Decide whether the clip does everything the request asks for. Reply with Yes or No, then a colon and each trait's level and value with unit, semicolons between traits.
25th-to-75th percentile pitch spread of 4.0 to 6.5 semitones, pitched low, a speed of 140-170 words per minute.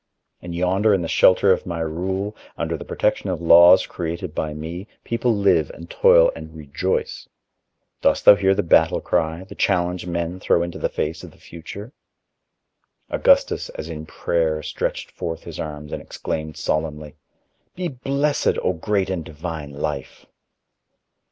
No: average, 3.1 semitones; very low, 85 Hz; average, 160 wpm